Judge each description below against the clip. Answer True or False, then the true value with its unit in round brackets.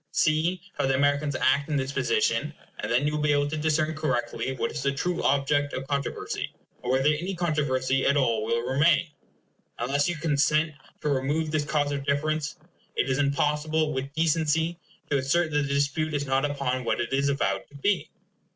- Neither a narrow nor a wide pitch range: False (2.3 semitones)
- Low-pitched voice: False (145 Hz)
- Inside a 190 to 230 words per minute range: True (195 wpm)